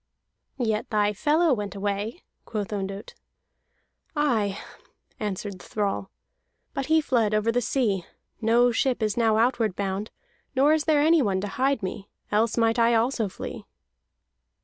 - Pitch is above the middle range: Yes, high, 225 Hz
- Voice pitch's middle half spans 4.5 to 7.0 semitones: No, average, 3.7 semitones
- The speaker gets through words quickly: No, average, 145 wpm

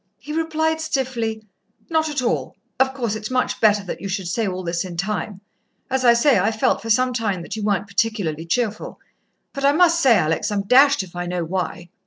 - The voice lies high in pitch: Yes, high, 220 Hz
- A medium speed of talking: No, fast, 215 wpm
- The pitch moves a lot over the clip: Yes, wide, 5.7 semitones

